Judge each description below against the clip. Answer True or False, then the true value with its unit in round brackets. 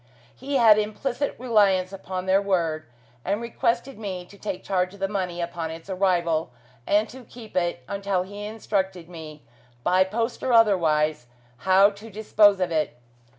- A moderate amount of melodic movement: True (3.3 semitones)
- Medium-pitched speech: False (195 Hz)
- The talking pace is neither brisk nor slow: True (160 wpm)